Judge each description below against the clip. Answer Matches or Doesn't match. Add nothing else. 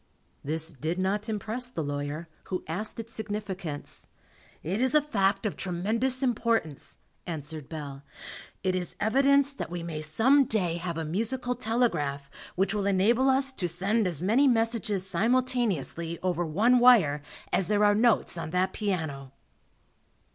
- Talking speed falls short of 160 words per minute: Matches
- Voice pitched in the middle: Doesn't match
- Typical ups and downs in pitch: Doesn't match